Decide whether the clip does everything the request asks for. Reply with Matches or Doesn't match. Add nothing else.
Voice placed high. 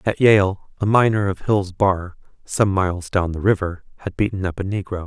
Doesn't match